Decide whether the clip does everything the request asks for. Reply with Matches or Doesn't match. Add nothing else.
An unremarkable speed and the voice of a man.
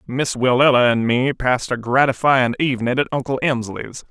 Matches